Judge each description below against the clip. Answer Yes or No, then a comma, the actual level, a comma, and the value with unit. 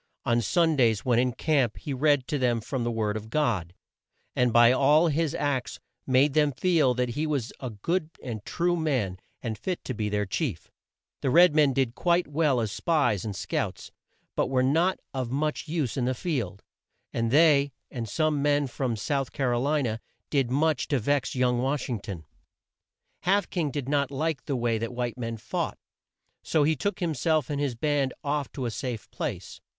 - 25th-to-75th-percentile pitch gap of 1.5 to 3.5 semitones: No, average, 4.2 semitones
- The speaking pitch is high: No, low, 135 Hz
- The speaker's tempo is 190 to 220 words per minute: Yes, average, 195 wpm